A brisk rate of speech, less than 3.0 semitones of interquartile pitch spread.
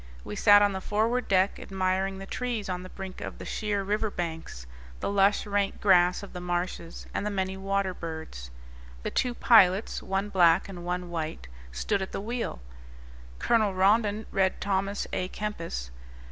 No: average, 175 wpm; narrow, 2.4 semitones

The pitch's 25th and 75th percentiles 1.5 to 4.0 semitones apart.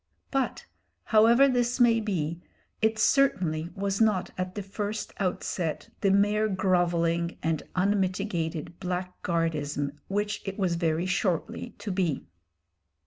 Yes: average, 3.7 semitones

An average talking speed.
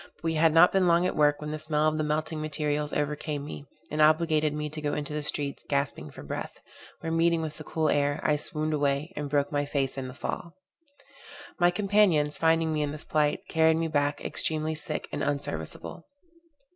No: fast, 210 wpm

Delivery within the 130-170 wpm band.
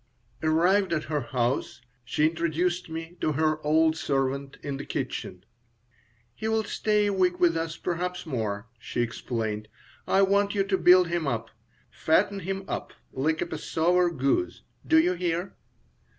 Yes: average, 150 wpm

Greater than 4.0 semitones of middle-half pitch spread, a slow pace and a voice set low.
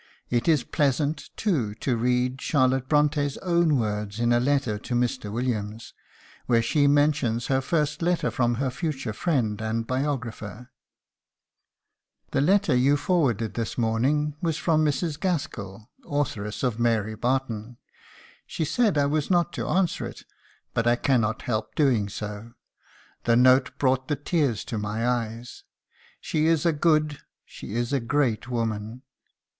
No: average, 4.4 semitones; average, 150 wpm; low, 130 Hz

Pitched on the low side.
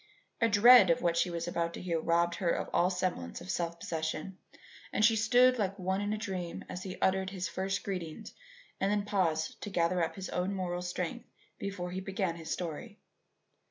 No: medium, 185 Hz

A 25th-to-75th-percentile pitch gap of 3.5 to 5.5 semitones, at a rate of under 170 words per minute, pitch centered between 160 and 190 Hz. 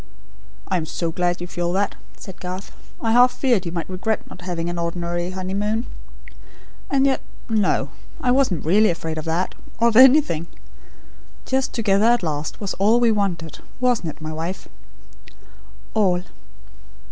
Yes: average, 4.8 semitones; average, 160 wpm; medium, 185 Hz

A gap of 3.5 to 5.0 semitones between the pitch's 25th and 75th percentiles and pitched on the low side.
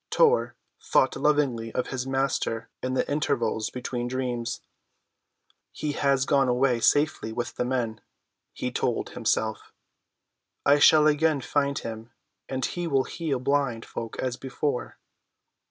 No: average, 3.0 semitones; low, 130 Hz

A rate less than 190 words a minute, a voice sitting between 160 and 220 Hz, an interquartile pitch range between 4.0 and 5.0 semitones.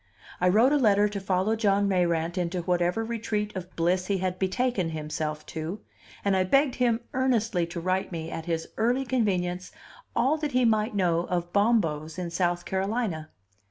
Yes: average, 175 wpm; high, 190 Hz; average, 4.3 semitones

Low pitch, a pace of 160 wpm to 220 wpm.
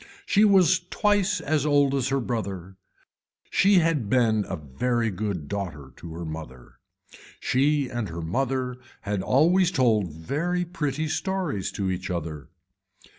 No: low, 125 Hz; average, 140 wpm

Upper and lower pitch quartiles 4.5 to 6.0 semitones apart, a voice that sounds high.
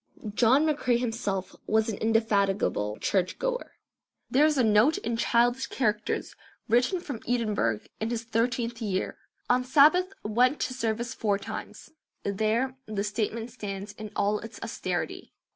No: average, 3.2 semitones; high, 230 Hz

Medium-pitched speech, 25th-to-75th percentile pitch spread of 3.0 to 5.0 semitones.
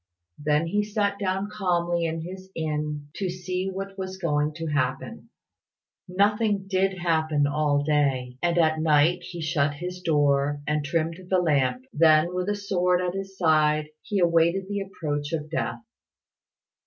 Yes: medium, 170 Hz; average, 3.8 semitones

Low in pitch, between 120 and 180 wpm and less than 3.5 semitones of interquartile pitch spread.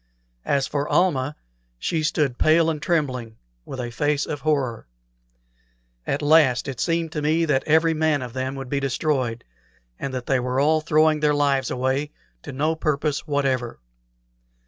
No: medium, 145 Hz; average, 165 wpm; average, 3.0 semitones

